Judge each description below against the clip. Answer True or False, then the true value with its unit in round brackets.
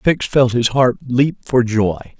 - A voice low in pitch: True (125 Hz)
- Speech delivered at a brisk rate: False (190 wpm)